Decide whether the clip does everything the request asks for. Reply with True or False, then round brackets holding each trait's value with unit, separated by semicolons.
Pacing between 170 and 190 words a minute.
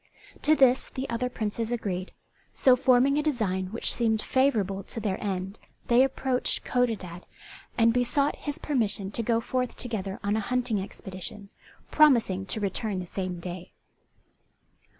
False (150 wpm)